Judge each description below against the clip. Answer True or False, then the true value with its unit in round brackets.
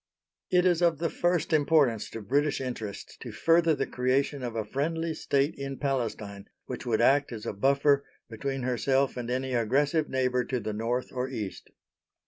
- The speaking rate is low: False (175 wpm)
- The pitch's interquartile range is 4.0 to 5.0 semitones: False (3.5 semitones)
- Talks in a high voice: False (135 Hz)